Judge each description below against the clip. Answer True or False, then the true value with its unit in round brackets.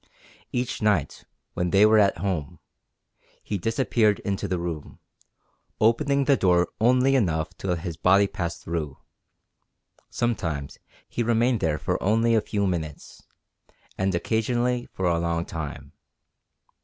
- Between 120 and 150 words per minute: True (135 wpm)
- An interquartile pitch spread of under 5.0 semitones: False (5.4 semitones)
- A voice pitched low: True (100 Hz)